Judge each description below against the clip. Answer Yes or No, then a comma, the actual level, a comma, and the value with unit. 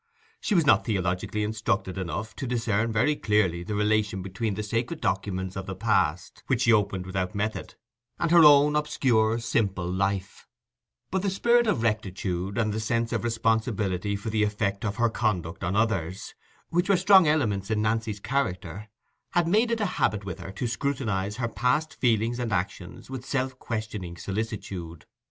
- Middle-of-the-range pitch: No, low, 110 Hz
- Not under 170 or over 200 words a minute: Yes, average, 175 wpm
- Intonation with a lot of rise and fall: No, average, 4.1 semitones